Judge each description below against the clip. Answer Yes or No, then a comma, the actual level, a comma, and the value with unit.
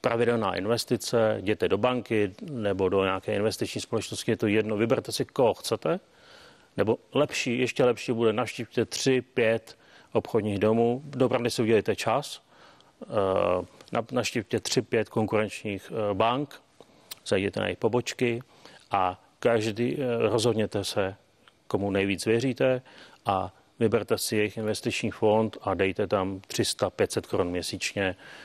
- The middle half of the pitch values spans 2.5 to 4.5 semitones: Yes, average, 2.8 semitones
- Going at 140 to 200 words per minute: No, average, 125 wpm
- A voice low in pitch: Yes, low, 115 Hz